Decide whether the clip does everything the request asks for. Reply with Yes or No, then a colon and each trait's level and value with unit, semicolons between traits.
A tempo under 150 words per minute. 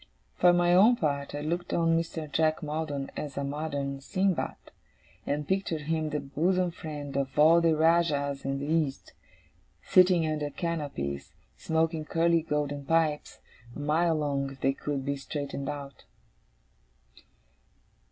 Yes: average, 140 wpm